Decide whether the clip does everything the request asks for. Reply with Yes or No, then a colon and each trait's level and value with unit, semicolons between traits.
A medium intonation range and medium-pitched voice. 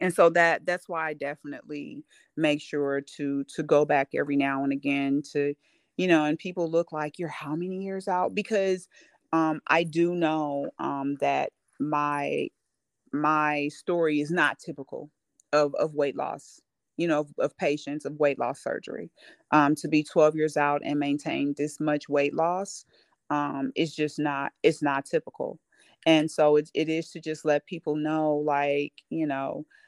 No: narrow, 2.2 semitones; medium, 150 Hz